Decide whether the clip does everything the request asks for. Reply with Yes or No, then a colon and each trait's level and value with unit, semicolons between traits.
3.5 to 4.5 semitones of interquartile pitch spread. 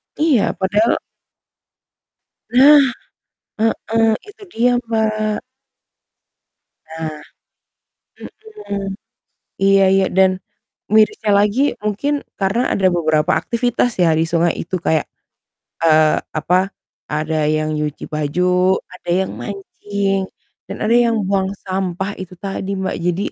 Yes: average, 3.9 semitones